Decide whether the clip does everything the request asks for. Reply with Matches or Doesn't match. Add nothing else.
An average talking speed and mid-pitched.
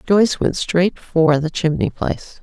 Matches